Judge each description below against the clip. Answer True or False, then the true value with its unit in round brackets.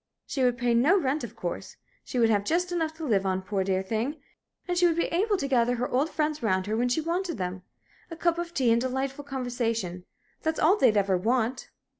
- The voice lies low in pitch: False (250 Hz)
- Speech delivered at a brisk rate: True (235 wpm)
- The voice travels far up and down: True (6.5 semitones)